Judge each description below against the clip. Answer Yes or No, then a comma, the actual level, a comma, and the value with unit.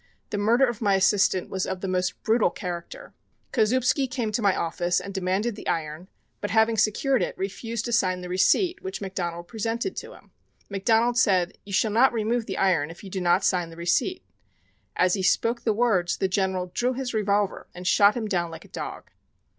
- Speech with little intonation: No, average, 4.0 semitones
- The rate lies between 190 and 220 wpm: Yes, average, 200 wpm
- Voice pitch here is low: No, high, 200 Hz